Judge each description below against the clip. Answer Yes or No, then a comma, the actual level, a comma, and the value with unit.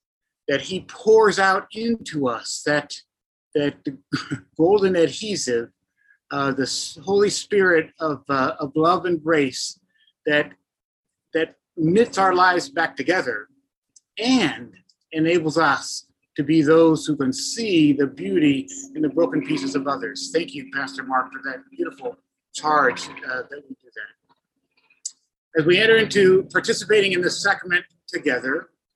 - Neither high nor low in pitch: Yes, medium, 170 Hz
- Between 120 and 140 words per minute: Yes, slow, 135 wpm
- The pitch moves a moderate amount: No, wide, 6.4 semitones